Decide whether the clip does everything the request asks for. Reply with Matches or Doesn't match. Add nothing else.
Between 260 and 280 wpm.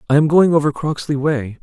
Doesn't match